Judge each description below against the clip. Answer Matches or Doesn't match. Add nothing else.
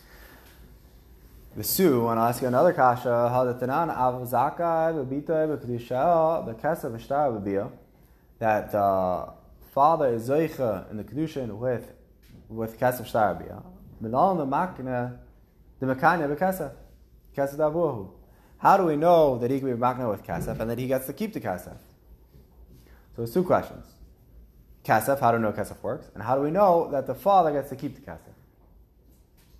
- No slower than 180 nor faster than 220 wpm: Doesn't match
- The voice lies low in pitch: Matches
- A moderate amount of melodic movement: Doesn't match